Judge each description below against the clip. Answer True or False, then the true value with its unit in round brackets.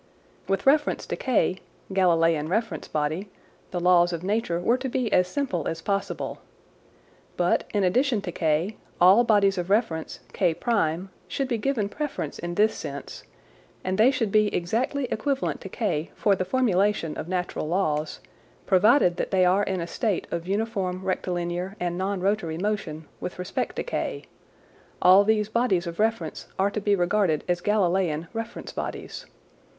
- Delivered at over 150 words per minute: True (160 wpm)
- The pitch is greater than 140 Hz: True (190 Hz)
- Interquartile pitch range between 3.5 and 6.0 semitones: True (3.8 semitones)